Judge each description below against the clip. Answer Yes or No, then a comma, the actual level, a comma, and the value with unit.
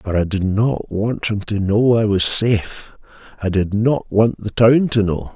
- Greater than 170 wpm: Yes, average, 200 wpm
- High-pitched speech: No, low, 105 Hz